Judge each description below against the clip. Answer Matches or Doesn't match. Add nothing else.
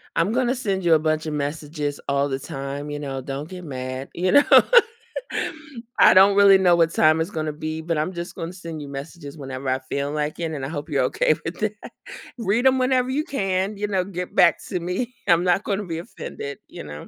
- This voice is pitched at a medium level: Matches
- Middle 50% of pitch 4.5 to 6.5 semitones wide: Matches